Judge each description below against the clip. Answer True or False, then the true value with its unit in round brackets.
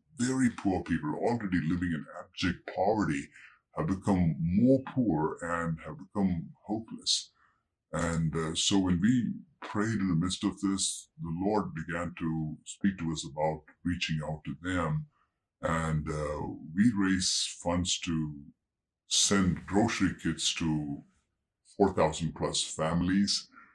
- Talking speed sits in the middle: False (130 wpm)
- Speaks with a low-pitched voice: True (85 Hz)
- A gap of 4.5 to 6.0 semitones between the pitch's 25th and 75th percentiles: False (3.8 semitones)